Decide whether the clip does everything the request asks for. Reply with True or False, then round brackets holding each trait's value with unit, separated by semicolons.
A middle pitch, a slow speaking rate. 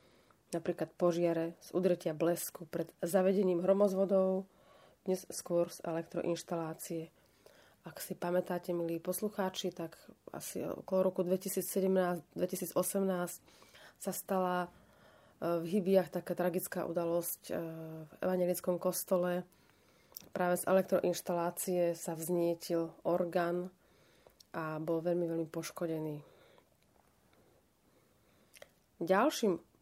True (180 Hz; 90 wpm)